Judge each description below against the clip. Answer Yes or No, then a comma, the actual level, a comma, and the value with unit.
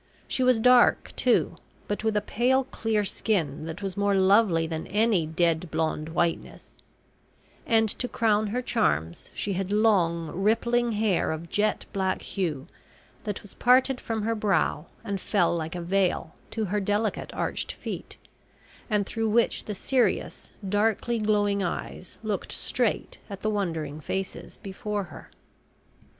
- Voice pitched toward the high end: Yes, high, 205 Hz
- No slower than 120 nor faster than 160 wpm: Yes, average, 150 wpm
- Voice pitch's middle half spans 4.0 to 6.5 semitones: Yes, average, 4.3 semitones